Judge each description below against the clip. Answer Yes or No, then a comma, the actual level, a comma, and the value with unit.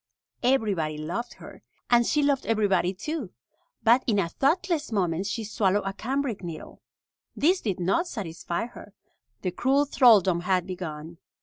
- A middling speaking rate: Yes, average, 145 wpm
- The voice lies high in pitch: Yes, high, 205 Hz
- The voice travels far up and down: Yes, wide, 6.4 semitones